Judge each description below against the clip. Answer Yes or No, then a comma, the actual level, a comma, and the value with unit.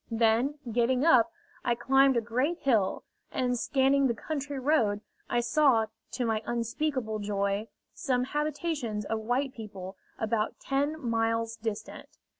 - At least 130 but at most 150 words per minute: Yes, slow, 135 wpm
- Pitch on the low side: No, high, 240 Hz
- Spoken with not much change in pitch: No, average, 3.7 semitones